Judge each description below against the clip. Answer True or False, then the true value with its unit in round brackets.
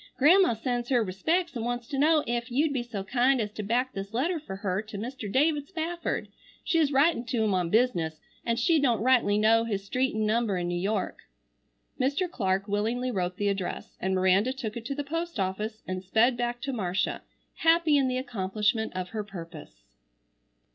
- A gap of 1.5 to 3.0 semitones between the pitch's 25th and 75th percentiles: False (5.1 semitones)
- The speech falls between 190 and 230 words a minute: True (195 wpm)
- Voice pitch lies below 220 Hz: False (230 Hz)